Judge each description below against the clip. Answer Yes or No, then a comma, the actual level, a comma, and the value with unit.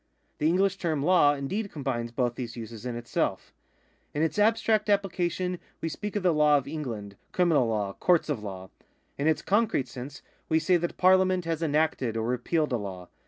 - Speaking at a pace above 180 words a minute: Yes, average, 190 wpm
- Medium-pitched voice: Yes, medium, 150 Hz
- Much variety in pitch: Yes, wide, 6.9 semitones